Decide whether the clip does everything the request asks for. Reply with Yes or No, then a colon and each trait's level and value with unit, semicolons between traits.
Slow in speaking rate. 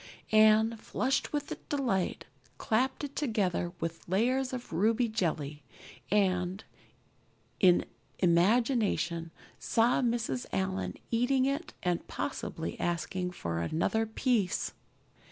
Yes: slow, 100 wpm